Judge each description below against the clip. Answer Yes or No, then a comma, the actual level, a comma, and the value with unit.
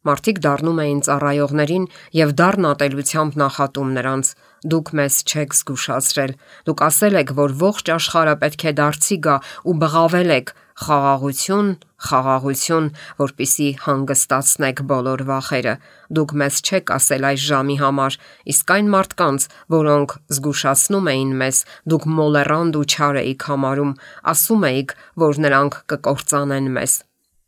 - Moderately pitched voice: Yes, medium, 145 Hz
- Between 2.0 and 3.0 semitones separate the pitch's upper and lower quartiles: Yes, average, 2.7 semitones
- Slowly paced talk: Yes, slow, 125 wpm